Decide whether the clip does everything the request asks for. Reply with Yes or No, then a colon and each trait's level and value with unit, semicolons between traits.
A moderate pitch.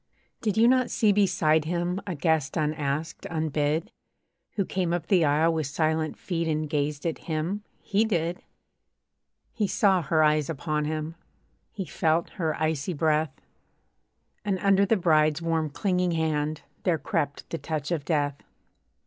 Yes: medium, 160 Hz